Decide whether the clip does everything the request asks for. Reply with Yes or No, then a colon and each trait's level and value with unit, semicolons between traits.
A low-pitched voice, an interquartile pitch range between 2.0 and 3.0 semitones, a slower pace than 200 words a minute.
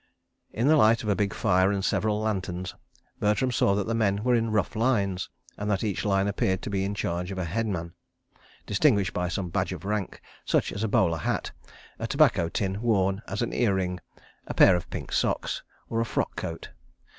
No: low, 100 Hz; narrow, 2.6 semitones; fast, 205 wpm